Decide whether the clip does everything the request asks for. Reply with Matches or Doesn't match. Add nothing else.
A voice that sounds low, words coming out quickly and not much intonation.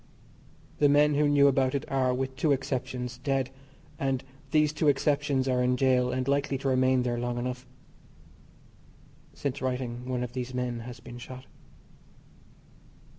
Doesn't match